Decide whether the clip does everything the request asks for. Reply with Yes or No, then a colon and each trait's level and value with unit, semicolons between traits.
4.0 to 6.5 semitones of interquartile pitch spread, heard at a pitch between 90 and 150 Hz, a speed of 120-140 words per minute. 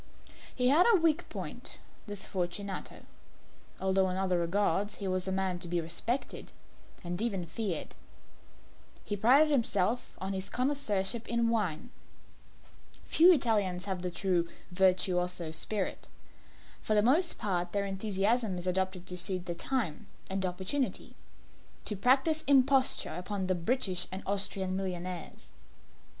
No: average, 4.3 semitones; high, 195 Hz; slow, 135 wpm